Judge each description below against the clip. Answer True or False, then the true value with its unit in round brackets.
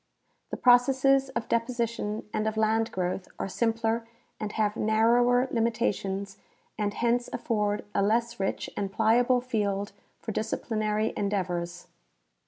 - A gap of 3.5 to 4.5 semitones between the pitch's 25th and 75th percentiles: False (2.5 semitones)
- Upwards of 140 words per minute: False (135 wpm)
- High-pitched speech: True (220 Hz)